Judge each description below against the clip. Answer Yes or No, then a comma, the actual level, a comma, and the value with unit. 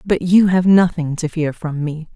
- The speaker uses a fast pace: Yes, fast, 225 wpm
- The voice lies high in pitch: No, medium, 165 Hz